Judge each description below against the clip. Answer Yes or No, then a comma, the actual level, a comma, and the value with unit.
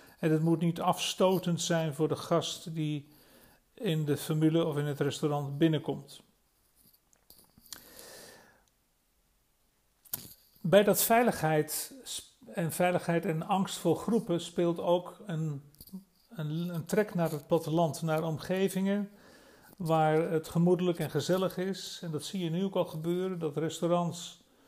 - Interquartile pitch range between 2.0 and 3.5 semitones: Yes, average, 2.7 semitones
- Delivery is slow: Yes, slow, 130 wpm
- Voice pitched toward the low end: No, medium, 170 Hz